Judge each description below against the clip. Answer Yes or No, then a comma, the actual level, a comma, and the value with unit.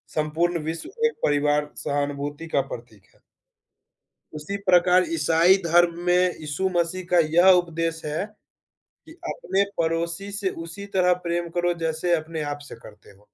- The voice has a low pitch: No, medium, 165 Hz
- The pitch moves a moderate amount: Yes, average, 3.0 semitones